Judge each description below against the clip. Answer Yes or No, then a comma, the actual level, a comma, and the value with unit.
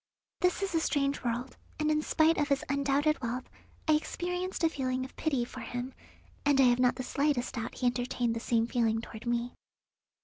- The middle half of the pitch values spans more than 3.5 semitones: Yes, average, 3.9 semitones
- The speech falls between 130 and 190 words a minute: No, average, 200 wpm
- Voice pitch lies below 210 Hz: No, very high, 265 Hz